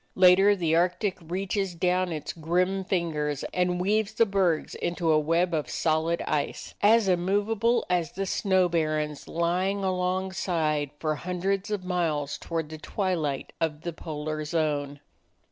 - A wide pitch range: No, average, 3.3 semitones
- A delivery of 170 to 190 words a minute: No, average, 145 wpm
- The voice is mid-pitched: Yes, medium, 175 Hz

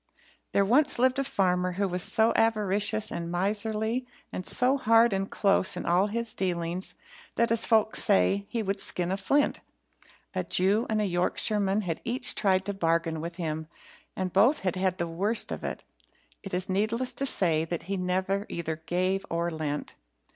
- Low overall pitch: No, high, 195 Hz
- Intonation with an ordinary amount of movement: Yes, average, 3.5 semitones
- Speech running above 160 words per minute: Yes, average, 180 wpm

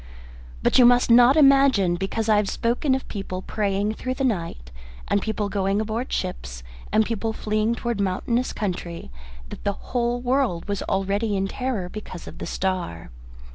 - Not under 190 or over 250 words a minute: No, average, 175 wpm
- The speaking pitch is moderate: No, high, 215 Hz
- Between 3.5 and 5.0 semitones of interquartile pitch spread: Yes, average, 3.9 semitones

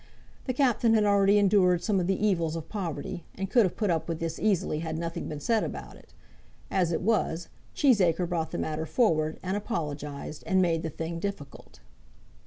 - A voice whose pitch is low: No, medium, 175 Hz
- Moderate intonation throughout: Yes, average, 4.0 semitones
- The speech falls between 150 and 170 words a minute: No, average, 195 wpm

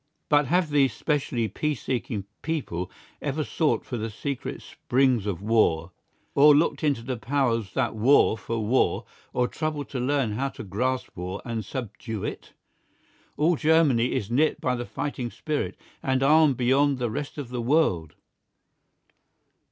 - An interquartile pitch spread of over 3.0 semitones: Yes, average, 4.3 semitones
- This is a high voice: No, low, 130 Hz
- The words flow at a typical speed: Yes, average, 155 wpm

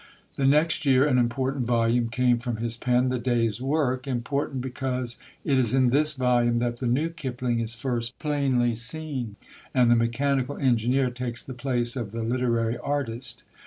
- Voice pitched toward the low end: Yes, low, 125 Hz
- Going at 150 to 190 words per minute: Yes, average, 170 wpm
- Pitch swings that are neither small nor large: No, narrow, 2.2 semitones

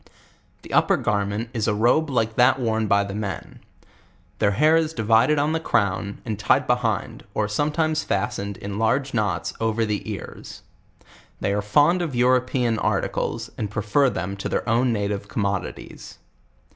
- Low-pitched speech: Yes, low, 110 Hz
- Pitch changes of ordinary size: Yes, average, 3.9 semitones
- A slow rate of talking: No, average, 170 wpm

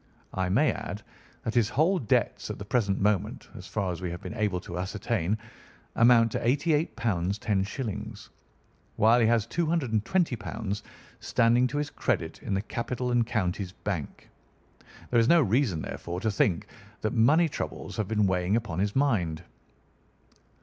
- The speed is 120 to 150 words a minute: No, average, 165 wpm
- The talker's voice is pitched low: Yes, low, 110 Hz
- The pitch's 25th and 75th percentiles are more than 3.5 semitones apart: Yes, average, 4.1 semitones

